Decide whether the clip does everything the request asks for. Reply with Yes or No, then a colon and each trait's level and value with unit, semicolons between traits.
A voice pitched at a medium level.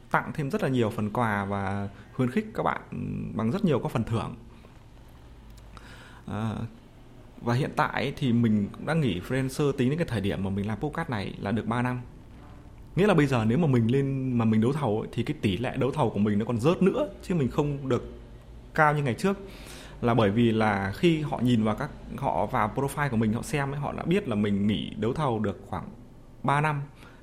No: low, 120 Hz